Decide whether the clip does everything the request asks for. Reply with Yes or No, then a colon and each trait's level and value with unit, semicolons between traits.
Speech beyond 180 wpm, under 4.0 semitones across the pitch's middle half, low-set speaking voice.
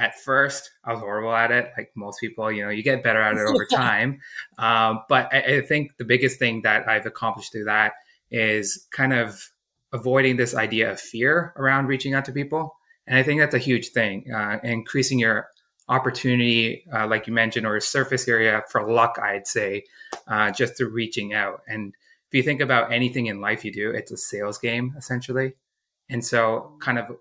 Yes: fast, 205 wpm; average, 3.0 semitones; low, 115 Hz